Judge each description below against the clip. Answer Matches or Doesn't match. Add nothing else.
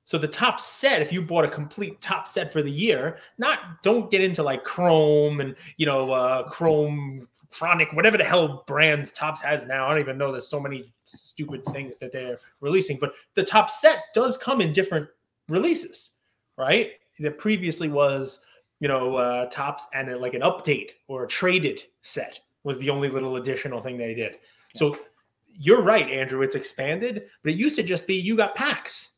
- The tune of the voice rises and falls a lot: Matches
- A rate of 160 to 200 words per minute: Matches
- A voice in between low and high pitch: Matches